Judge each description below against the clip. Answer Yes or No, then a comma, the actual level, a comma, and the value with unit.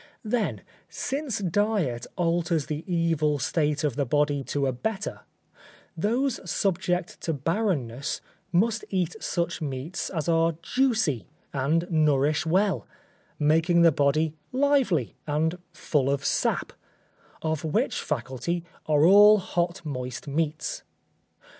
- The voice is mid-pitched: Yes, medium, 165 Hz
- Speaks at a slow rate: Yes, slow, 120 wpm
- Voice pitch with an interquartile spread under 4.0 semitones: No, average, 4.3 semitones